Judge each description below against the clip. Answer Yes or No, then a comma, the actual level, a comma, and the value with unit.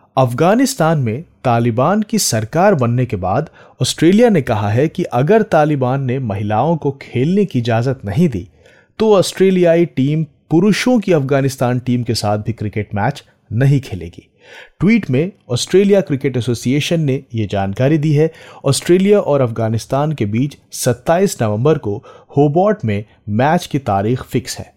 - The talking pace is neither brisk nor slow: Yes, average, 150 wpm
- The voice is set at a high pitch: No, low, 135 Hz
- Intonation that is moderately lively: No, wide, 6.3 semitones